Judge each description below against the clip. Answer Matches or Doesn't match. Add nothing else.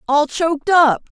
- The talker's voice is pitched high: Matches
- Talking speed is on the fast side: Doesn't match